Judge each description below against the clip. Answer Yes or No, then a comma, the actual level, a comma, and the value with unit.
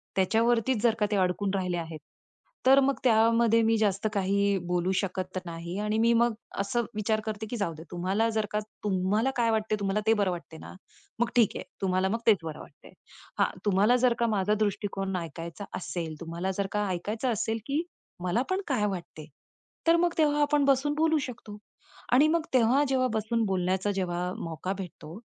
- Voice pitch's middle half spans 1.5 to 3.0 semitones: No, average, 3.9 semitones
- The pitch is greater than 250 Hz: No, high, 210 Hz